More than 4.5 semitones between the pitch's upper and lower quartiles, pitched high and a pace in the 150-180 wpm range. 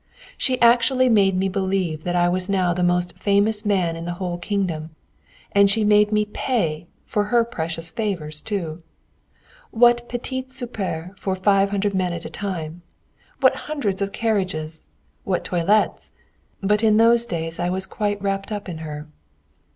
No: average, 3.3 semitones; high, 195 Hz; average, 165 wpm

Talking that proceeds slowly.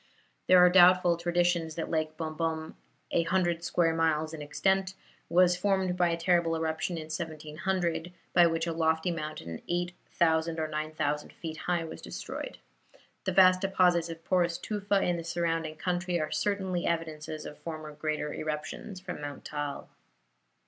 No: average, 155 wpm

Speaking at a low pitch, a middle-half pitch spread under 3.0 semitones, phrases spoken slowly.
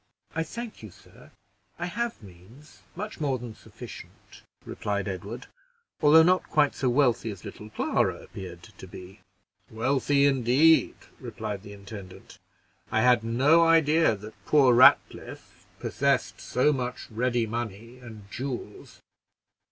No: low, 120 Hz; wide, 5.6 semitones; slow, 130 wpm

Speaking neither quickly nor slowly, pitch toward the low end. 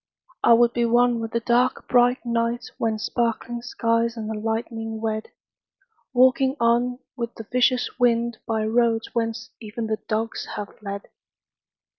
No: average, 150 wpm; high, 230 Hz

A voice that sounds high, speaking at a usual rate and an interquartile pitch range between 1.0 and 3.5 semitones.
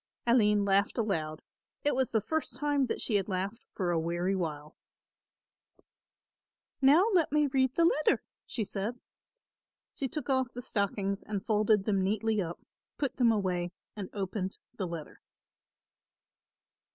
No: high, 210 Hz; average, 145 wpm; average, 5.3 semitones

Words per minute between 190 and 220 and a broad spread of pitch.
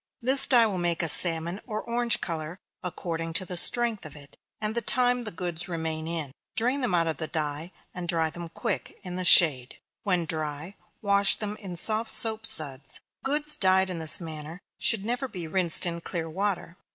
No: average, 195 wpm; average, 4.9 semitones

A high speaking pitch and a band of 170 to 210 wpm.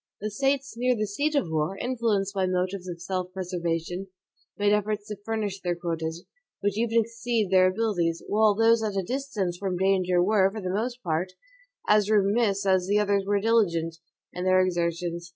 Yes: high, 195 Hz; average, 180 wpm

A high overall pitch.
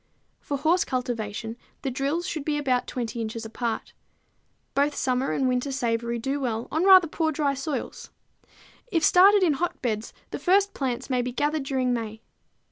Yes: very high, 265 Hz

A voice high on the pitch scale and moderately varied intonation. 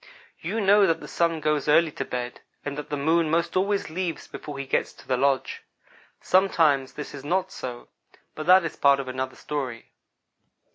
No: medium, 150 Hz; average, 3.8 semitones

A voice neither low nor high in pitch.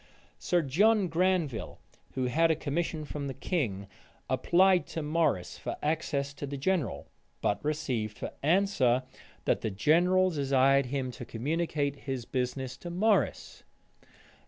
Yes: medium, 145 Hz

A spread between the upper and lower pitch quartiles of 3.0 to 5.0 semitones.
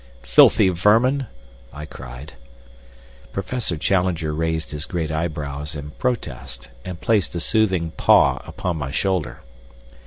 Yes: average, 4.1 semitones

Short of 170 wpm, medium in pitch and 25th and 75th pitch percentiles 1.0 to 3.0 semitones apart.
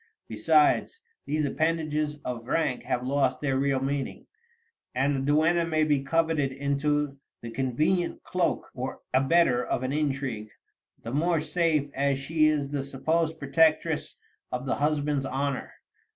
Yes: average, 140 wpm; medium, 145 Hz; average, 2.7 semitones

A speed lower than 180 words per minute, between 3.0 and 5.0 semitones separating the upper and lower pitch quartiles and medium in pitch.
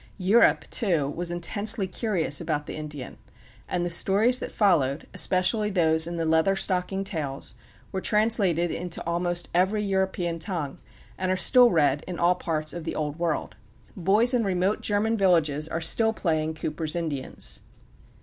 Yes: average, 160 wpm; average, 3.6 semitones; medium, 175 Hz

